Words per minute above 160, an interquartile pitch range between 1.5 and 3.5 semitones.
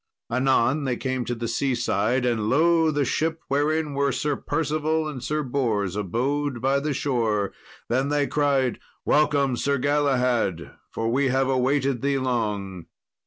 No: average, 150 wpm; average, 3.2 semitones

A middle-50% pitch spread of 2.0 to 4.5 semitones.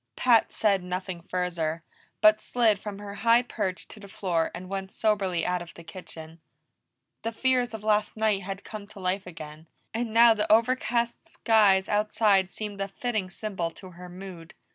Yes: average, 3.2 semitones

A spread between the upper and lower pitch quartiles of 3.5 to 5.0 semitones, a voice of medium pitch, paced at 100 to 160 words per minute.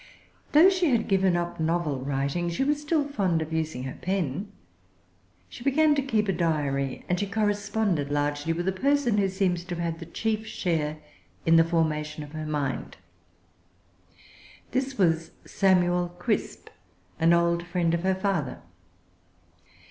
Yes: average, 4.3 semitones; medium, 175 Hz; average, 155 wpm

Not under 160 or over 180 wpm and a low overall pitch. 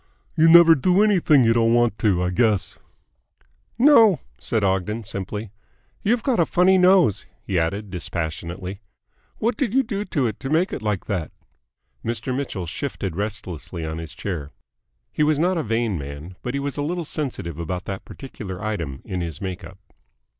Yes: average, 175 wpm; low, 110 Hz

